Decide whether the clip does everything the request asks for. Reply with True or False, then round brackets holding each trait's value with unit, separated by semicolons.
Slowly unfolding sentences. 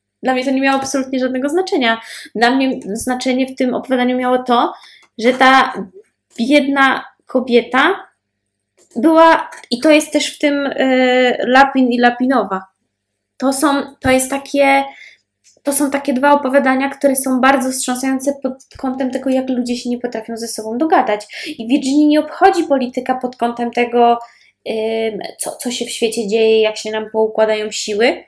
False (160 wpm)